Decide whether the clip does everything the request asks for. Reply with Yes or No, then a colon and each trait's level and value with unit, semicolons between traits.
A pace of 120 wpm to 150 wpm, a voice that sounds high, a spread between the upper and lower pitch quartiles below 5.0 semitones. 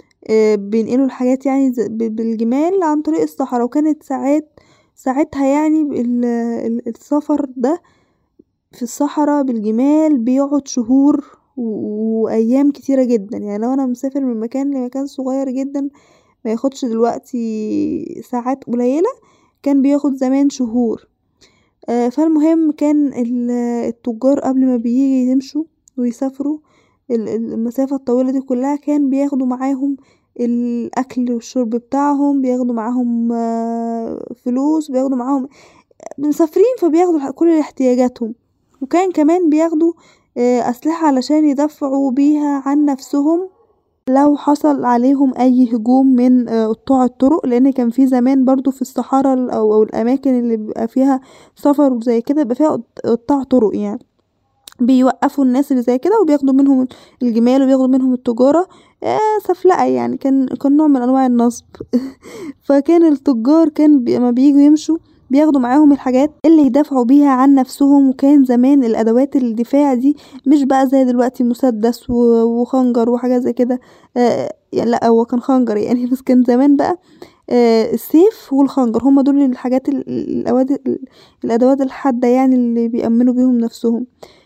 Yes: average, 125 wpm; very high, 265 Hz; average, 2.8 semitones